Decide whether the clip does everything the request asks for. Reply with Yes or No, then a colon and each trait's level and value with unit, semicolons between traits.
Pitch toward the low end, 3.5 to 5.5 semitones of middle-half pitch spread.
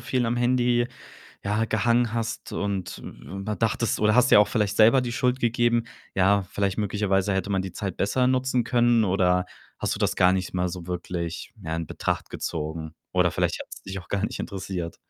Yes: low, 105 Hz; average, 4.2 semitones